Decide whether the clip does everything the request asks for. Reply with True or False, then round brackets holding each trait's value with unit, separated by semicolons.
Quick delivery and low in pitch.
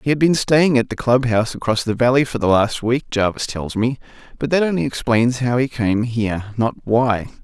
True (225 wpm; 120 Hz)